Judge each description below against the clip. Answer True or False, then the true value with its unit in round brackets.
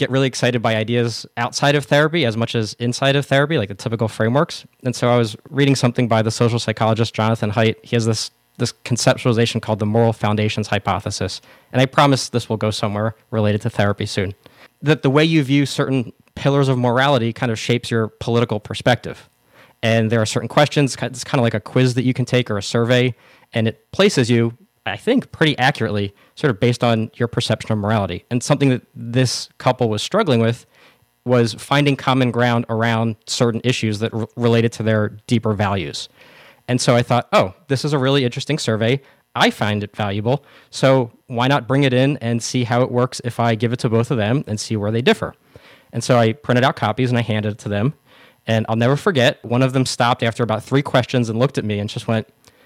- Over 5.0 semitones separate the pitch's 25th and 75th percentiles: False (2.7 semitones)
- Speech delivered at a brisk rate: True (220 wpm)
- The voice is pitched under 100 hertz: False (120 Hz)